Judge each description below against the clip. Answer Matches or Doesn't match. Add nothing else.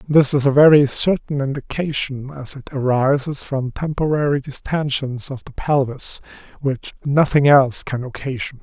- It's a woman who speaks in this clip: Doesn't match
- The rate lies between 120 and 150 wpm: Matches